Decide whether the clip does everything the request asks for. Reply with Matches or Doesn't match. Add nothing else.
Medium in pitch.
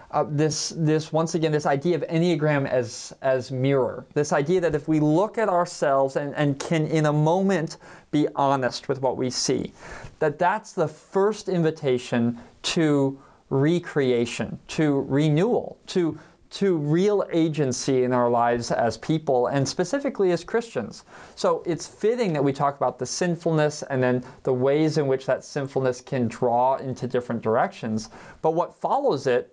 Matches